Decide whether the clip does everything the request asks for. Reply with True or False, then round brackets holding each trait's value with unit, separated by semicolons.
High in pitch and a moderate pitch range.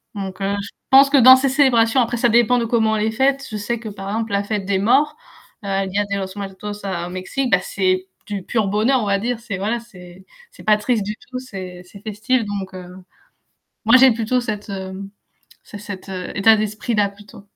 True (210 Hz; 3.3 semitones)